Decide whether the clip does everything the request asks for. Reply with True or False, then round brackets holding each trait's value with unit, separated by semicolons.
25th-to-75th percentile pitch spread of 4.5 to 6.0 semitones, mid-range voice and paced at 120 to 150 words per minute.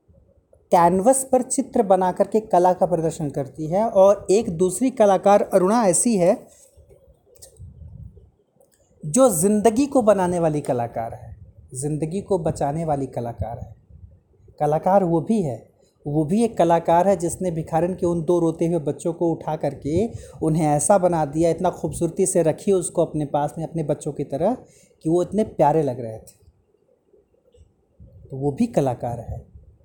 False (5.2 semitones; 170 Hz; 160 wpm)